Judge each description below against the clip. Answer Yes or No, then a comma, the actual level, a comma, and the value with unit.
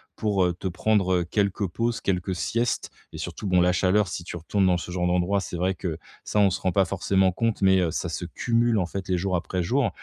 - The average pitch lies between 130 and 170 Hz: No, very low, 95 Hz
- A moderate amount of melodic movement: No, narrow, 2.3 semitones